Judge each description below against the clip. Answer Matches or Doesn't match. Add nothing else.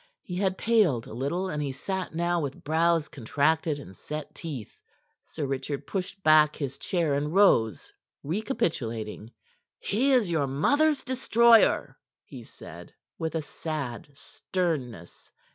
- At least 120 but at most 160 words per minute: Matches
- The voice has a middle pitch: Matches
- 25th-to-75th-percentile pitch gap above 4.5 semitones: Matches